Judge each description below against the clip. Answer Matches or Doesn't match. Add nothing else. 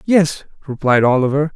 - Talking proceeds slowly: Matches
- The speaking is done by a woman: Doesn't match